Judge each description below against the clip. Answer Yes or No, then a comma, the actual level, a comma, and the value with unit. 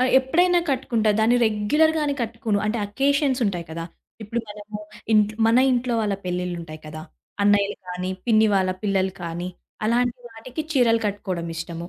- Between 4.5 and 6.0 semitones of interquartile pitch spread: Yes, average, 5.1 semitones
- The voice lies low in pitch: No, high, 215 Hz